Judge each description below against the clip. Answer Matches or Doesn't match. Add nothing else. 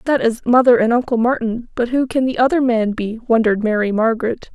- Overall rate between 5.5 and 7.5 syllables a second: Matches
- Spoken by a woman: Matches